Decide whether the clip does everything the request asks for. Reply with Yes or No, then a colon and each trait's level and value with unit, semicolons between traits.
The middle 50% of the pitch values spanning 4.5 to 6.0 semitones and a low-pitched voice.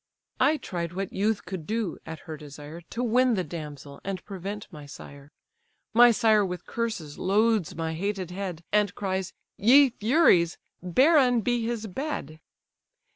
No: wide, 5.5 semitones; high, 195 Hz